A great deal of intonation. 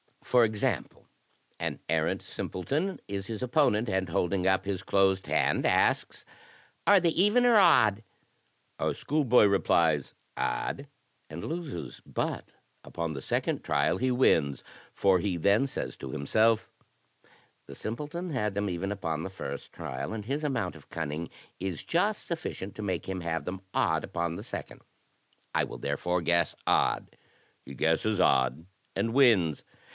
Yes: wide, 6.8 semitones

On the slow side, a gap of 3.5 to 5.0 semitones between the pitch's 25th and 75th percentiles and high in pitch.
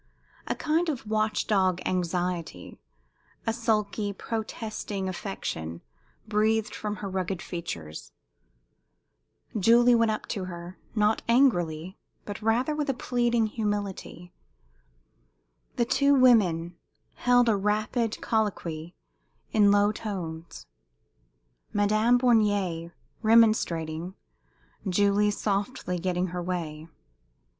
Yes: slow, 100 wpm; average, 4.0 semitones; high, 205 Hz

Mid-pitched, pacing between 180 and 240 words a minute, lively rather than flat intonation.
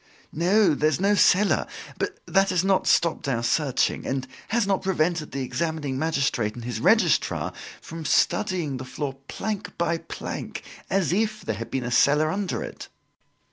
No: medium, 165 Hz; average, 165 wpm; wide, 6.1 semitones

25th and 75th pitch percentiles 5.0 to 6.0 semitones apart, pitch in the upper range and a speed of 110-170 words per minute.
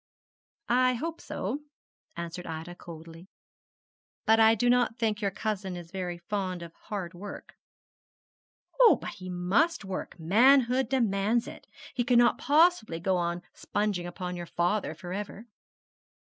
Yes: average, 5.3 semitones; high, 200 Hz; average, 140 wpm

